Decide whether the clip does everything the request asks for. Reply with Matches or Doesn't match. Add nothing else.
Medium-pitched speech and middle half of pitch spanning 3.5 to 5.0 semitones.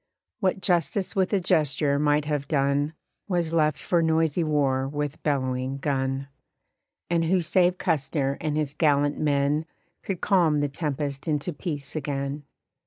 Doesn't match